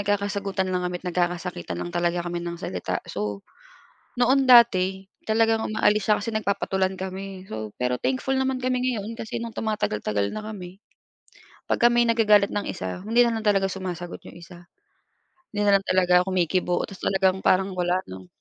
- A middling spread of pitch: Yes, average, 3.5 semitones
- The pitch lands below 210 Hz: Yes, high, 190 Hz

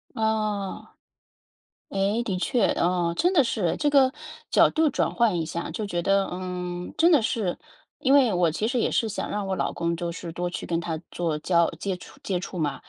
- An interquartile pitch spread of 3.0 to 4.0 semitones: No, average, 4.6 semitones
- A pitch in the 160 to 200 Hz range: Yes, high, 190 Hz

